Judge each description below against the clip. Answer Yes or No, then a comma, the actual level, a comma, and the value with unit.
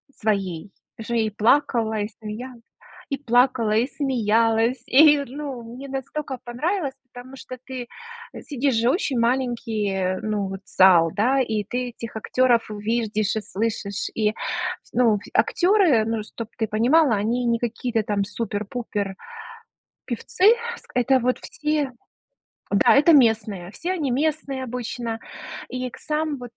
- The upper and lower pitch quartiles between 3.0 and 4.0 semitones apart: Yes, average, 3.6 semitones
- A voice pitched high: Yes, high, 235 Hz